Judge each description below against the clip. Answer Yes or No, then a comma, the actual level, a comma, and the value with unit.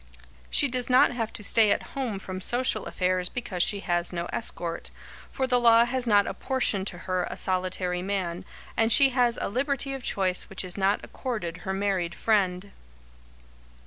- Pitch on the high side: Yes, high, 200 Hz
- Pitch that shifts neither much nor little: Yes, average, 4.8 semitones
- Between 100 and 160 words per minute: No, average, 175 wpm